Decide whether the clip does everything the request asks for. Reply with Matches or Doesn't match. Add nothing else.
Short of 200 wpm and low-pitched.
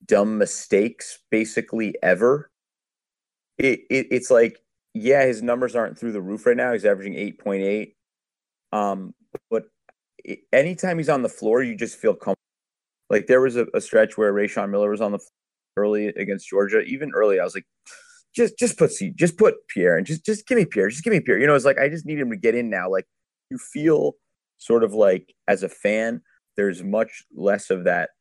Doesn't match